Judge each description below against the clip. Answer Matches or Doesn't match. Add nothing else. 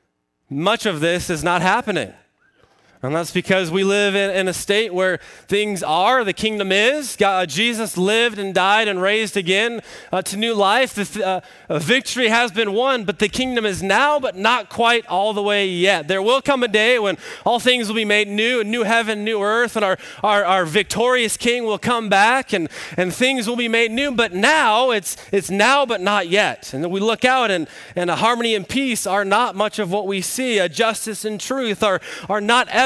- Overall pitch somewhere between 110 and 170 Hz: Doesn't match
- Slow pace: Doesn't match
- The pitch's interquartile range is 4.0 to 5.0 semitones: Doesn't match